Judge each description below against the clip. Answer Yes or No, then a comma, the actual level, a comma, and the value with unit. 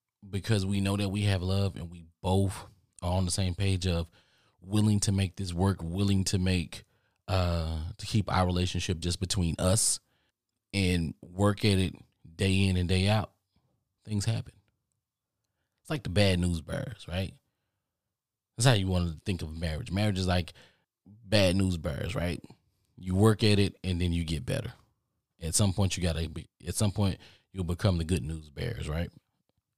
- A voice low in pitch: Yes, very low, 95 Hz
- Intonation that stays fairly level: No, average, 3.0 semitones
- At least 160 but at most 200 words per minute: Yes, average, 180 wpm